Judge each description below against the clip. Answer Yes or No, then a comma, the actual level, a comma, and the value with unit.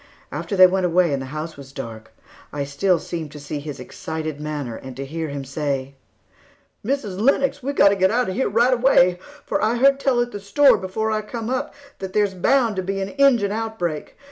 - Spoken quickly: Yes, fast, 220 wpm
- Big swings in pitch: Yes, wide, 7.4 semitones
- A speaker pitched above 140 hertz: Yes, high, 190 Hz